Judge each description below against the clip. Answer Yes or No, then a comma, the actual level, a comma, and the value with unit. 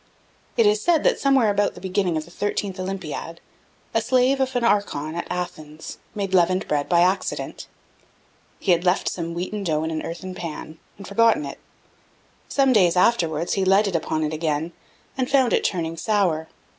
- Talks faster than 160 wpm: Yes, average, 180 wpm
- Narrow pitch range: No, average, 4.1 semitones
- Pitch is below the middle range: No, medium, 185 Hz